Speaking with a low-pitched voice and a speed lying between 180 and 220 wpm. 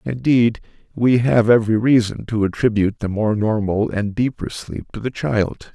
No: low, 110 Hz; average, 165 wpm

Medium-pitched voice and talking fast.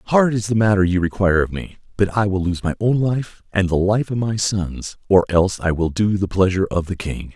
No: low, 100 Hz; fast, 255 wpm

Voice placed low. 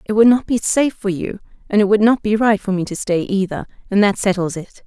No: high, 200 Hz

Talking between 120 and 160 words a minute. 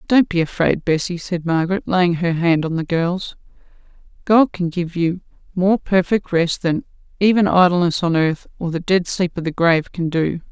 No: average, 190 wpm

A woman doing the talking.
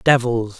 No: male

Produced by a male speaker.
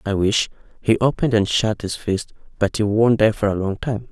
Yes: male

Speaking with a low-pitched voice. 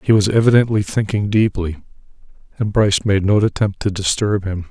Yes: low, 100 Hz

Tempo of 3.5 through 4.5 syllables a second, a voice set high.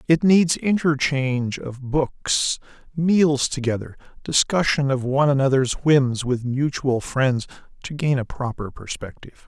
No: 4.2 syllables/s; low, 135 Hz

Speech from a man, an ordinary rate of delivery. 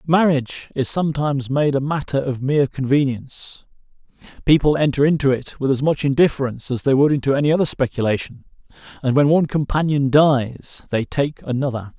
Yes: male; average, 160 wpm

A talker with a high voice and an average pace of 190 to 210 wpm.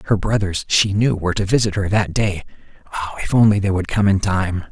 No: low, 100 Hz; fast, 205 wpm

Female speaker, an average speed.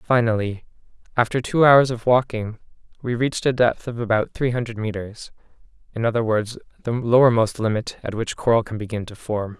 No: male; average, 175 wpm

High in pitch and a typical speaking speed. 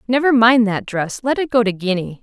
No: high, 225 Hz; fast, 245 wpm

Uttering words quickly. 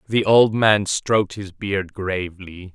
No: average, 155 wpm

